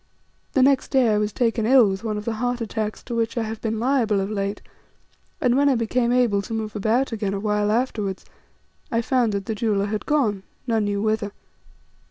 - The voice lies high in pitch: Yes, high, 220 Hz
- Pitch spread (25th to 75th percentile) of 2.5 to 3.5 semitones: Yes, average, 2.8 semitones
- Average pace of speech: No, fast, 215 wpm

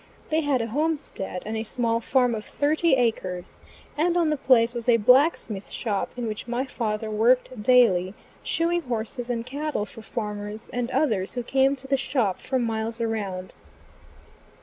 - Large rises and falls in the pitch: No, average, 3.7 semitones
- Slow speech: No, average, 170 wpm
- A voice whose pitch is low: No, high, 235 Hz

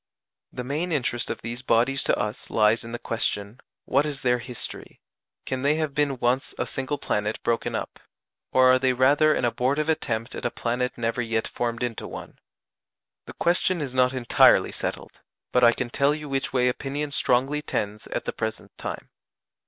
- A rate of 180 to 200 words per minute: Yes, average, 185 wpm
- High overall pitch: No, low, 125 Hz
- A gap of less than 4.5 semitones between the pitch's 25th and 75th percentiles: Yes, average, 3.1 semitones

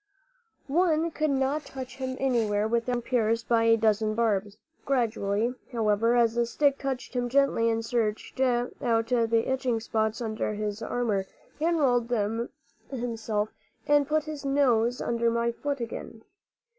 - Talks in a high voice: Yes, high, 235 Hz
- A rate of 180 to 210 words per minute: No, average, 145 wpm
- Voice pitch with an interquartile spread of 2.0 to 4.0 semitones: Yes, average, 2.9 semitones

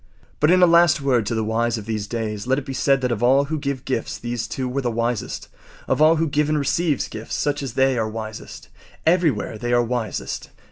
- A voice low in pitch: Yes, low, 125 Hz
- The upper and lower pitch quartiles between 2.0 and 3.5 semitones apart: No, average, 4.1 semitones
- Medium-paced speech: No, fast, 235 wpm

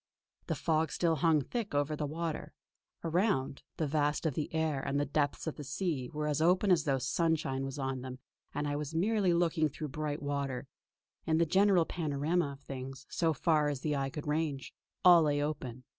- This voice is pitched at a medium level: Yes, medium, 150 Hz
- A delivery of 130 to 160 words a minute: No, average, 200 wpm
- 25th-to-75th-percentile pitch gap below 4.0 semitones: Yes, average, 2.7 semitones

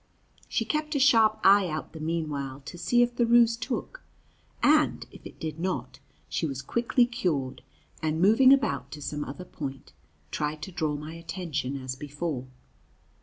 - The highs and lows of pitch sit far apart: Yes, wide, 8.0 semitones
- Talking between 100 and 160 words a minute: No, average, 170 wpm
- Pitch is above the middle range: No, medium, 165 Hz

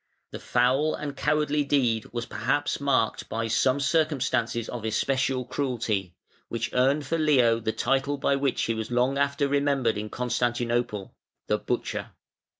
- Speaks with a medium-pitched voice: No, low, 125 Hz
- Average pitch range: Yes, average, 3.4 semitones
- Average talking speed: Yes, average, 150 wpm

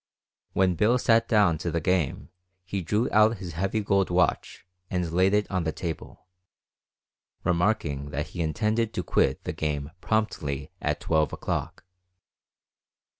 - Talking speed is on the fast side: No, average, 145 wpm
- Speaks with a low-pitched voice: Yes, very low, 90 Hz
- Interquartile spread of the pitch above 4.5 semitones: Yes, average, 4.9 semitones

